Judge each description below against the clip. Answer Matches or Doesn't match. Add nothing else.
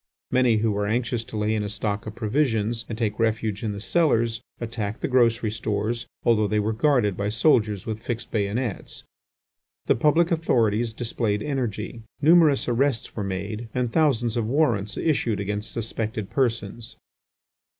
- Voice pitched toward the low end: Matches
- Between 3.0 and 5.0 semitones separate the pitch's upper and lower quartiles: Doesn't match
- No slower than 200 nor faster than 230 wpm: Doesn't match